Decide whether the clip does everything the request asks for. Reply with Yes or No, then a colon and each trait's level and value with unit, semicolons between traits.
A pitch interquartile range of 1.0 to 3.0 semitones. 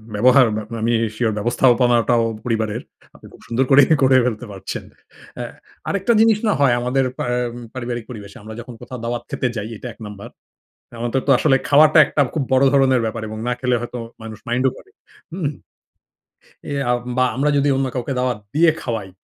Yes: average, 2.7 semitones